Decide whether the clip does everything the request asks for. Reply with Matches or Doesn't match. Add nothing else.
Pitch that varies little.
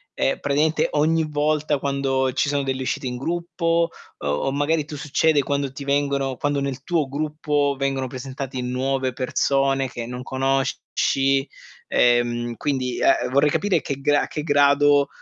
Matches